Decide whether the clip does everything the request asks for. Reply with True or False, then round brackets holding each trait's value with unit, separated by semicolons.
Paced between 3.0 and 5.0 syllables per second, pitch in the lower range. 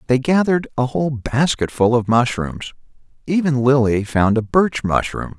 True (4.6 syllables/s; 130 Hz)